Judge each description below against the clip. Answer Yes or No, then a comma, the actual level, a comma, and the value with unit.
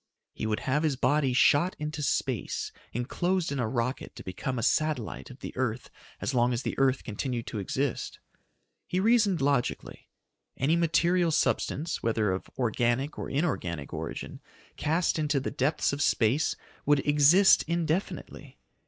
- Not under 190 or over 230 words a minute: No, average, 155 wpm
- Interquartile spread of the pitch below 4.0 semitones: No, average, 4.4 semitones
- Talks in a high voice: No, medium, 140 Hz